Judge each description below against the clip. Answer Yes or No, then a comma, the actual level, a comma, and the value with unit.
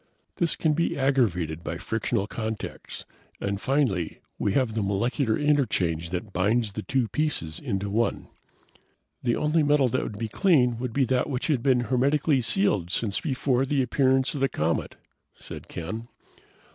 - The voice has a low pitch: Yes, low, 120 Hz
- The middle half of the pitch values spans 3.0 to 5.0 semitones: No, wide, 5.4 semitones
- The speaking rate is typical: Yes, average, 160 wpm